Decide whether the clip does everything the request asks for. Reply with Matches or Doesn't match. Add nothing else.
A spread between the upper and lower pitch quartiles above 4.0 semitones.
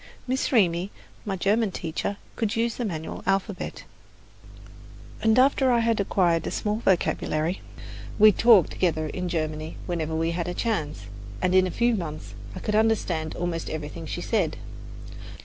Matches